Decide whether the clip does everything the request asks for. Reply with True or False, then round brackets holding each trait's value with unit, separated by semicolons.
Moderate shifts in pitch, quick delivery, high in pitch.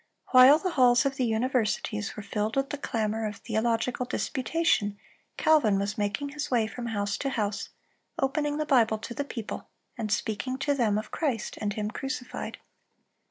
False (4.2 semitones; 170 wpm; 235 Hz)